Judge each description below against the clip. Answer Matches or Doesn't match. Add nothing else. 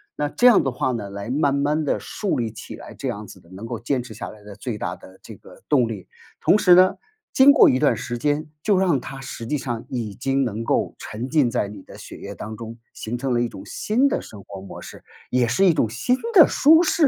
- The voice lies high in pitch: Doesn't match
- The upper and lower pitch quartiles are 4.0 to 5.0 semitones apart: Doesn't match